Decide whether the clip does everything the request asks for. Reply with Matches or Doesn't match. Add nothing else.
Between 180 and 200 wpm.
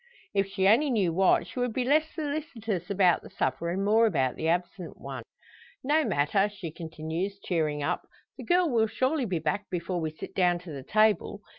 Matches